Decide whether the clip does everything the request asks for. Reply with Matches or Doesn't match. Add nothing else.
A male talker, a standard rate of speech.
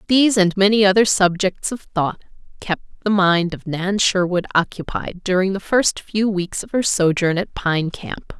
Doesn't match